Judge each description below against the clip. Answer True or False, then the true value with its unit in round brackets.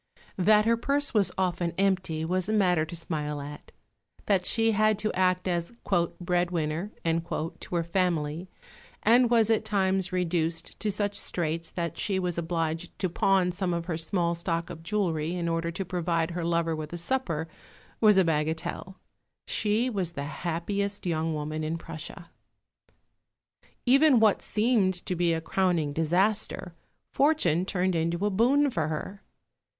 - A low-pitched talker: False (175 Hz)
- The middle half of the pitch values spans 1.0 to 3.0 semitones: False (3.4 semitones)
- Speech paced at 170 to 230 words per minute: False (155 wpm)